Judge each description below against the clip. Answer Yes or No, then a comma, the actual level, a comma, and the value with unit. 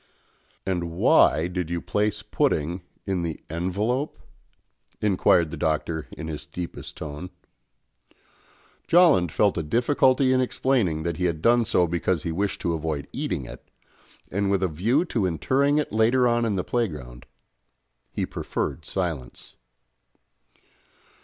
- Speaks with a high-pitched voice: No, very low, 90 Hz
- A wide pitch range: Yes, wide, 6.2 semitones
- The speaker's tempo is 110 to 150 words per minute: Yes, average, 140 wpm